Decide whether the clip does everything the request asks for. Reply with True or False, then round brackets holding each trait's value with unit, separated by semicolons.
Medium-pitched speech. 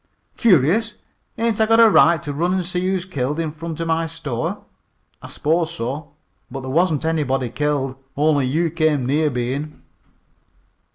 True (155 Hz)